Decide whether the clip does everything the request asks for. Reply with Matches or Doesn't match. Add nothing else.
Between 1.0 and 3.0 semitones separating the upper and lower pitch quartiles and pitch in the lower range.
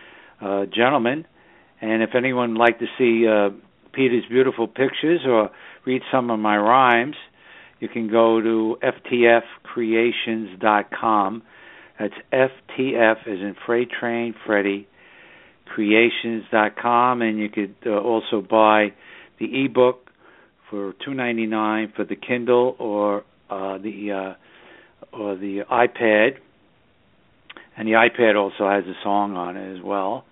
Matches